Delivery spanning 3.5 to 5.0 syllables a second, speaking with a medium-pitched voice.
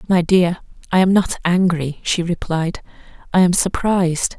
Yes: 4.5 syllables/s; medium, 175 Hz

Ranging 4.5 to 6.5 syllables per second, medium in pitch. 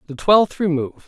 Yes: 5.6 syllables/s; medium, 165 Hz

